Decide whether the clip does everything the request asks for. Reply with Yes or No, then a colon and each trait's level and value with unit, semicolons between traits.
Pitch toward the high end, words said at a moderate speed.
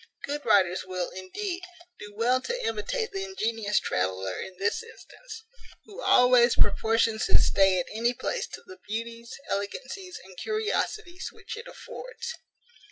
Yes: high, 235 Hz; average, 145 wpm